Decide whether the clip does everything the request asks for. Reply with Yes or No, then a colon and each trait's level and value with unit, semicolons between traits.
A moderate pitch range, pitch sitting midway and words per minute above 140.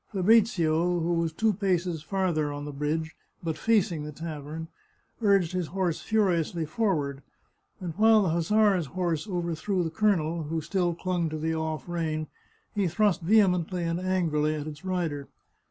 Yes: average, 3.1 semitones; medium, 170 Hz; average, 155 wpm